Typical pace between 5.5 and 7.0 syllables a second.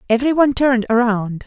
Yes: 6.4 syllables/s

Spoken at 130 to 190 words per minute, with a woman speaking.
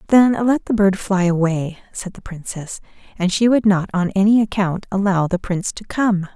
No: average, 200 wpm; female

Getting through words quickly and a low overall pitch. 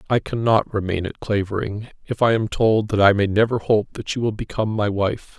Yes: fast, 225 wpm; low, 105 Hz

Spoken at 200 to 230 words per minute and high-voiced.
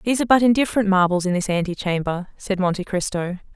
Yes: fast, 205 wpm; high, 195 Hz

